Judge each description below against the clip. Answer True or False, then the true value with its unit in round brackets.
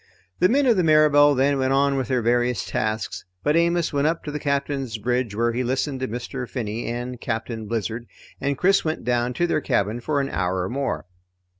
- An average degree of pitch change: True (3.7 semitones)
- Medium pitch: False (130 Hz)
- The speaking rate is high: True (210 wpm)